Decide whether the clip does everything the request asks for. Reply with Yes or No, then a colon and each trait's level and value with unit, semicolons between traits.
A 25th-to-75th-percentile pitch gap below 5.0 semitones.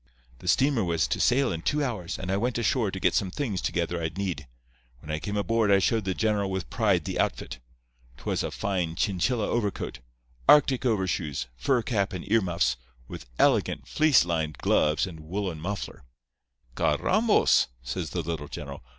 No: wide, 5.6 semitones